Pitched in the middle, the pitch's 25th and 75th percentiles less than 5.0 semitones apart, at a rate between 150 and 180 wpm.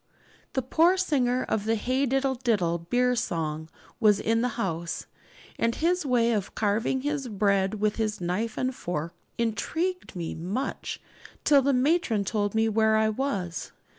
No: high, 225 Hz; average, 4.6 semitones; average, 160 wpm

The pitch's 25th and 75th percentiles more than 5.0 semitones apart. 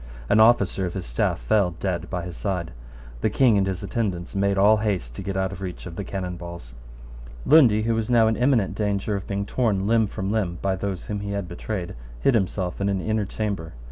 No: average, 3.0 semitones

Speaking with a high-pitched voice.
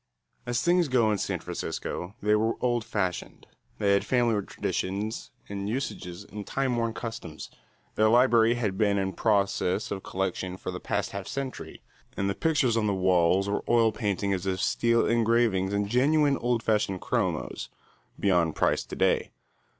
No: low, 105 Hz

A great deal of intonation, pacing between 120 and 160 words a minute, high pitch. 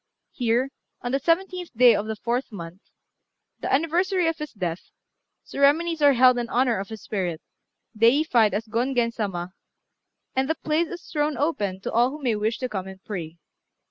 No: wide, 6.0 semitones; average, 175 wpm; high, 245 Hz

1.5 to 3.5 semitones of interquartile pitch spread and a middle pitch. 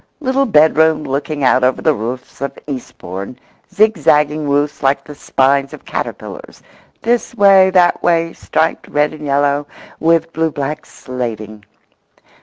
Yes: average, 3.2 semitones; medium, 150 Hz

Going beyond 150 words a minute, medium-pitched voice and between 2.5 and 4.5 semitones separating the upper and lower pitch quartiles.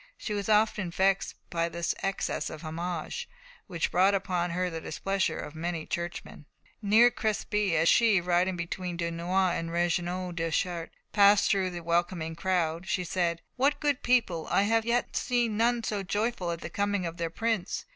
Yes: average, 175 wpm; medium, 180 Hz; average, 3.4 semitones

